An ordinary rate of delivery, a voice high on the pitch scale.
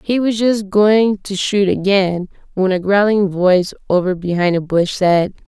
Yes: average, 170 wpm; high, 195 Hz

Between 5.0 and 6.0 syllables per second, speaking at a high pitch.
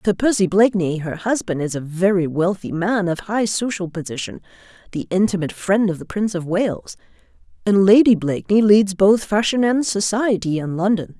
Yes: 5.3 syllables/s; high, 195 Hz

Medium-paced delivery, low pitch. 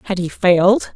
No: average, 190 wpm; medium, 185 Hz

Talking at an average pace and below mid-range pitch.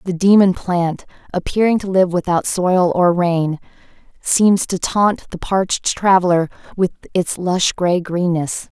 No: average, 145 wpm; medium, 180 Hz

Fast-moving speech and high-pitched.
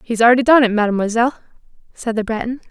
No: average, 180 wpm; high, 230 Hz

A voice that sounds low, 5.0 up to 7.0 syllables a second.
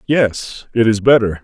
No: low, 115 Hz; 4.0 syllables/s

